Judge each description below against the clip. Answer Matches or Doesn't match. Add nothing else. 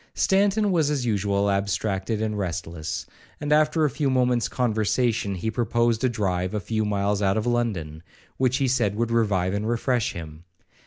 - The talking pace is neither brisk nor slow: Matches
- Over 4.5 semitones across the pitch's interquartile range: Doesn't match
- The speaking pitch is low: Matches